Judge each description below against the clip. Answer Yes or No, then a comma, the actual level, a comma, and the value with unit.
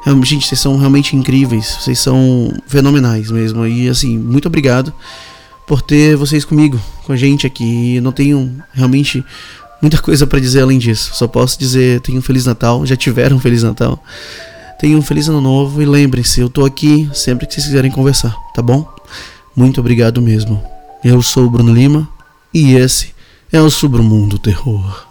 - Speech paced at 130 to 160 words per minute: No, average, 175 wpm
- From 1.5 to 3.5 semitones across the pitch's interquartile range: Yes, average, 3.1 semitones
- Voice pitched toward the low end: Yes, low, 130 Hz